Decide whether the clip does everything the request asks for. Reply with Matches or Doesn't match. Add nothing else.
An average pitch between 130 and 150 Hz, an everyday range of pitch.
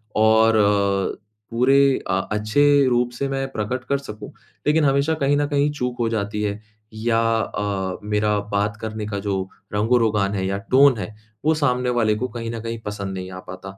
Doesn't match